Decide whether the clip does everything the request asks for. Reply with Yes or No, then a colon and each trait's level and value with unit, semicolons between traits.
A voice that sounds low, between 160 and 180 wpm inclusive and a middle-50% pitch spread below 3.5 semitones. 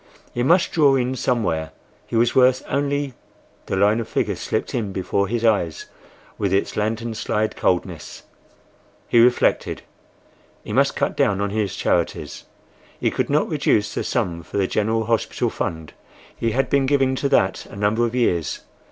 No: low, 110 Hz; average, 165 wpm; average, 3.9 semitones